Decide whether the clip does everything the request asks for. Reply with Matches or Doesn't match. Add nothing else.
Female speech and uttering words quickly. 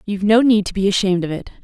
Matches